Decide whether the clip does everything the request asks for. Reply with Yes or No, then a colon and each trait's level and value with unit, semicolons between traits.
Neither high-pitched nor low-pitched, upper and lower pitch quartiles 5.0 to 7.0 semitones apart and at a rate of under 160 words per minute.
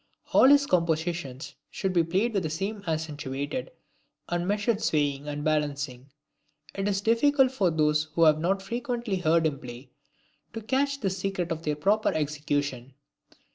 Yes: medium, 170 Hz; wide, 5.5 semitones; average, 150 wpm